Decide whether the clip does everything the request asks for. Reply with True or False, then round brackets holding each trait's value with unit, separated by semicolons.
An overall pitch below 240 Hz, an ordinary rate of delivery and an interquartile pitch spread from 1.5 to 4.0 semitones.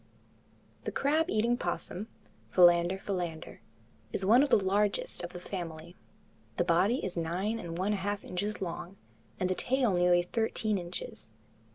True (190 Hz; 150 wpm; 3.3 semitones)